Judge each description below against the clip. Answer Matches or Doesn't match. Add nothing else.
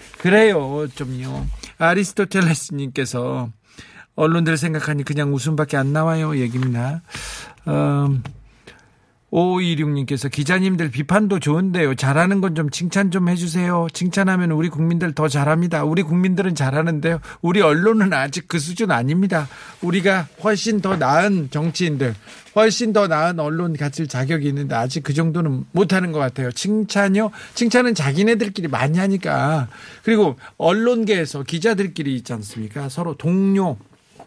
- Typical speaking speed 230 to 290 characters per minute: Doesn't match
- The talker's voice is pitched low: Doesn't match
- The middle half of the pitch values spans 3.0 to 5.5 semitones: Matches